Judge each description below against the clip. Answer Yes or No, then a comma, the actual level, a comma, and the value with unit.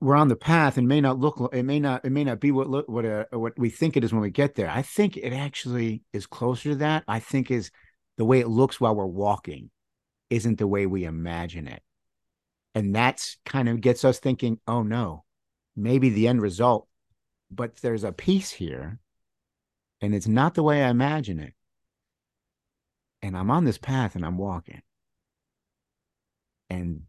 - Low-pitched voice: Yes, low, 120 Hz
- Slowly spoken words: No, average, 190 wpm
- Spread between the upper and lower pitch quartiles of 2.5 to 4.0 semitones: No, average, 4.6 semitones